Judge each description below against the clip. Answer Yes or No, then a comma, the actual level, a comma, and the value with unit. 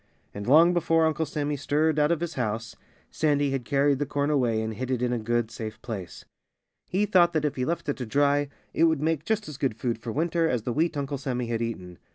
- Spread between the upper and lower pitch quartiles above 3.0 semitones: Yes, average, 4.9 semitones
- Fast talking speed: Yes, fast, 240 wpm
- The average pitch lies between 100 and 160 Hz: Yes, medium, 140 Hz